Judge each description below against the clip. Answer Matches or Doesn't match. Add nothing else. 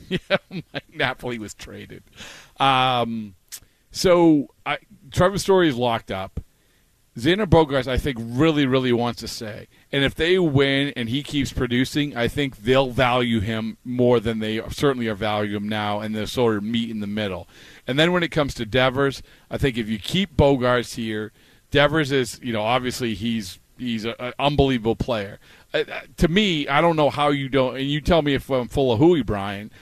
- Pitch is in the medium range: Doesn't match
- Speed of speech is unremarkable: Matches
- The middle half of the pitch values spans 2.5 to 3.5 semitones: Doesn't match